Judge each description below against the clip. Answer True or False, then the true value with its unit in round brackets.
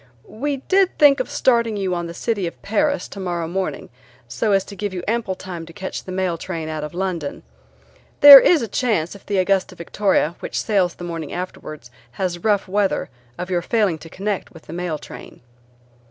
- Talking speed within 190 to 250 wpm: True (195 wpm)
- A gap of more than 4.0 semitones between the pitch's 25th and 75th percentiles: False (3.7 semitones)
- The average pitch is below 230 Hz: True (190 Hz)